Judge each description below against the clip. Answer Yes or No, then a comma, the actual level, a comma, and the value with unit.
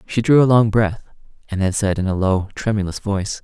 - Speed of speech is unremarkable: No, fast, 225 wpm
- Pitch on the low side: Yes, low, 105 Hz